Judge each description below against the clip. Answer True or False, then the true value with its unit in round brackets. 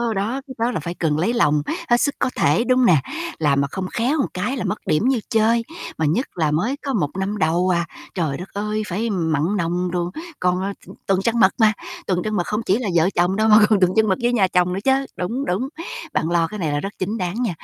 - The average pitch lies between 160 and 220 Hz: True (190 Hz)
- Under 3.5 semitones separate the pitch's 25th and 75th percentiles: False (4.8 semitones)